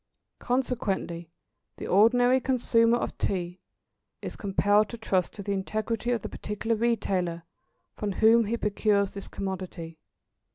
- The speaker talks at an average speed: No, slow, 130 wpm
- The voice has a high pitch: Yes, high, 210 Hz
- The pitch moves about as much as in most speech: Yes, average, 3.4 semitones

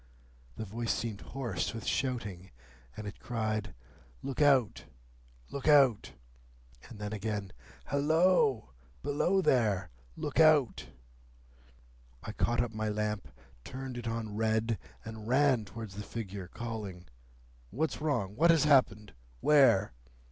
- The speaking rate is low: Yes, slow, 125 wpm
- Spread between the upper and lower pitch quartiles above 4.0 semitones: Yes, average, 4.5 semitones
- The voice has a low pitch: Yes, low, 115 Hz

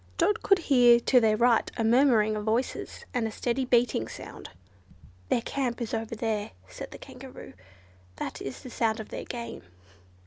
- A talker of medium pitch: No, high, 235 Hz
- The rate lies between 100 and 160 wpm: No, average, 175 wpm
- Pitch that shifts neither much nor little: No, narrow, 2.2 semitones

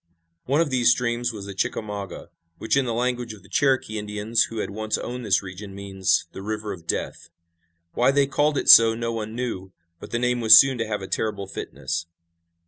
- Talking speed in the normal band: No, fast, 210 wpm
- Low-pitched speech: Yes, low, 110 Hz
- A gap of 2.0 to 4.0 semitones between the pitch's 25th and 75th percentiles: Yes, average, 3.6 semitones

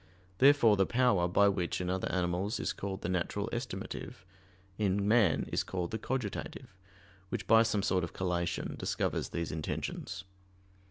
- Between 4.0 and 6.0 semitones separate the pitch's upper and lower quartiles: No, average, 3.2 semitones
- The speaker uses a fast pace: No, average, 155 wpm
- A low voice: Yes, very low, 95 Hz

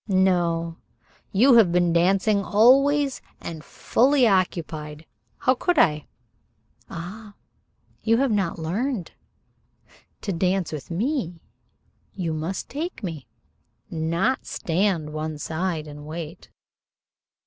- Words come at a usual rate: No, slow, 105 wpm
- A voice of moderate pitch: Yes, medium, 180 Hz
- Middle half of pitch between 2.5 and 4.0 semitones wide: No, wide, 5.4 semitones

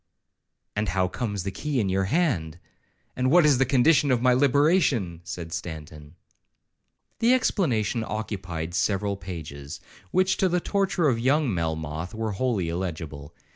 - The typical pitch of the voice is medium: No, low, 105 Hz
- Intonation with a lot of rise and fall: Yes, wide, 8.5 semitones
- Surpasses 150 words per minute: No, average, 145 wpm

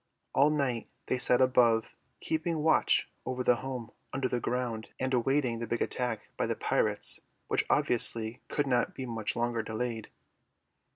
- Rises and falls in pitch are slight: Yes, narrow, 2.2 semitones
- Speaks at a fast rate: No, average, 160 wpm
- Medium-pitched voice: No, low, 125 Hz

